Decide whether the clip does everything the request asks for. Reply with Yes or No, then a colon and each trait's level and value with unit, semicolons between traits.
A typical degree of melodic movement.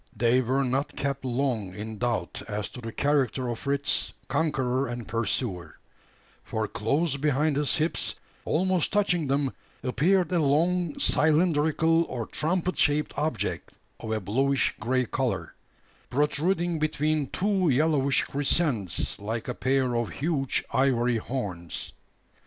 Yes: average, 4.3 semitones